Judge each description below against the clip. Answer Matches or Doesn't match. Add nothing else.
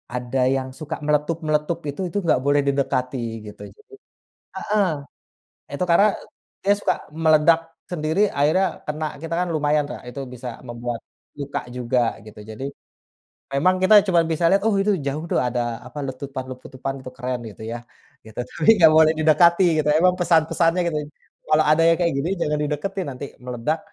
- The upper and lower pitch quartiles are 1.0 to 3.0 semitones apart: Doesn't match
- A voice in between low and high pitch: Matches